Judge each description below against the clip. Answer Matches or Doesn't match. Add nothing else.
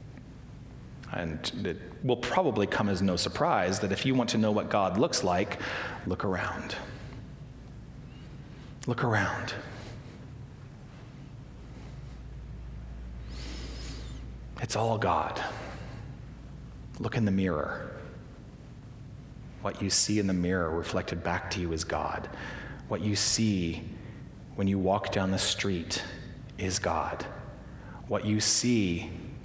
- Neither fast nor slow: Doesn't match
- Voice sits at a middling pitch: Doesn't match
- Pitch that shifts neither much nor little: Doesn't match